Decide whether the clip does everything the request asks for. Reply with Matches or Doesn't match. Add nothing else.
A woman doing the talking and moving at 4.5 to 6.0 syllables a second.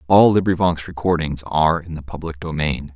Doesn't match